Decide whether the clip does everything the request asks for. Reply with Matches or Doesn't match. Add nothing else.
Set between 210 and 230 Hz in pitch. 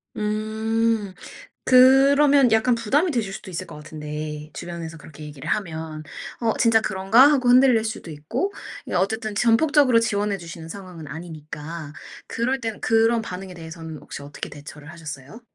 Doesn't match